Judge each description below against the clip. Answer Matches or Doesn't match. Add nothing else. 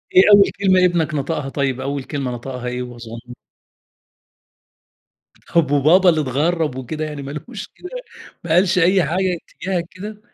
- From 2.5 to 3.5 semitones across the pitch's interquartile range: Doesn't match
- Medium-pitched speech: Matches